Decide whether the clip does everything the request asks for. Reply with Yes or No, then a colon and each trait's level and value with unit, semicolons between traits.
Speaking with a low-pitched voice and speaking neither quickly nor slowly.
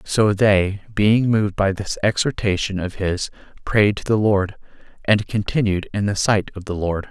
Yes: low, 100 Hz; average, 175 wpm